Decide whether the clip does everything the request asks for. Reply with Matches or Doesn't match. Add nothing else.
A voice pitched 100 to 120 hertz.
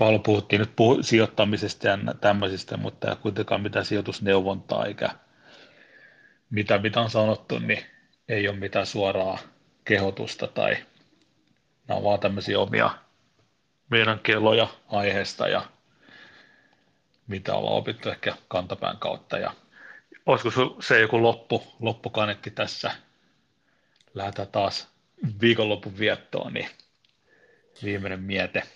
Matches